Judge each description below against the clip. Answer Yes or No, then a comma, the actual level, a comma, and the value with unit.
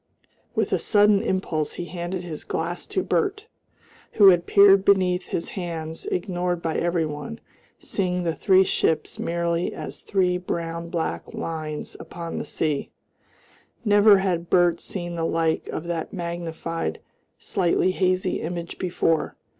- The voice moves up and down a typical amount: No, narrow, 2.0 semitones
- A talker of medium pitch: Yes, medium, 175 Hz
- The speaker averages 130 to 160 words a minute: Yes, average, 140 wpm